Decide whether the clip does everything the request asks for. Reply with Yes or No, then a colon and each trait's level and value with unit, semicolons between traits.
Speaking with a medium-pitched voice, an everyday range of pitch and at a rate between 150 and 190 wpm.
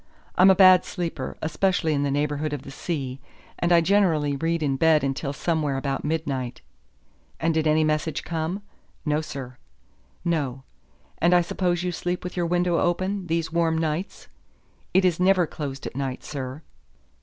Yes: medium, 160 Hz; average, 3.6 semitones; average, 165 wpm